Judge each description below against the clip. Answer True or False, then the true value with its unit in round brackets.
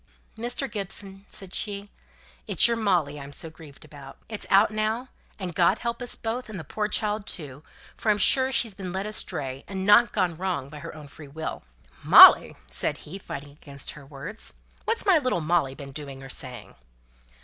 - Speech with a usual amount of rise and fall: False (6.8 semitones)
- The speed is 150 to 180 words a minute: False (190 wpm)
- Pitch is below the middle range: False (190 Hz)